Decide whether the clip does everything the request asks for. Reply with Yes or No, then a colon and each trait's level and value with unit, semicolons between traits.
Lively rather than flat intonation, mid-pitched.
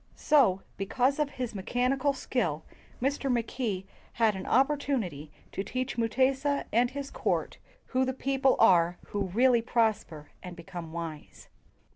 No: wide, 6.1 semitones; high, 235 Hz